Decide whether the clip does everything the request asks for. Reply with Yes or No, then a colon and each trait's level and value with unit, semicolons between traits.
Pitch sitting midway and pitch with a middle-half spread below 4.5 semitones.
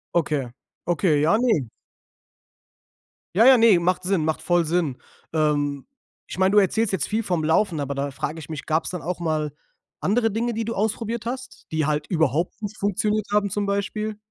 No: medium, 180 Hz; wide, 5.4 semitones